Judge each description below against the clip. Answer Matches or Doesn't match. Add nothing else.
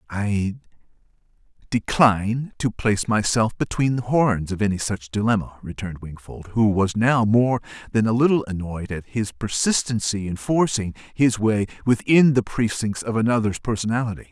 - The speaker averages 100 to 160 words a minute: Matches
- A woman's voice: Doesn't match